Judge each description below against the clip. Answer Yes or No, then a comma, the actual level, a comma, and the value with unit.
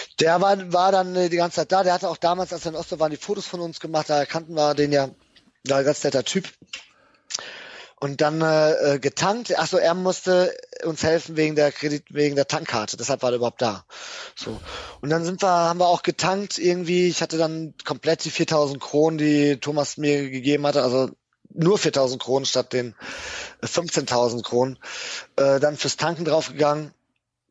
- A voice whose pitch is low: No, medium, 155 Hz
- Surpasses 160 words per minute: Yes, fast, 190 wpm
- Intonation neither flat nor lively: Yes, average, 3.6 semitones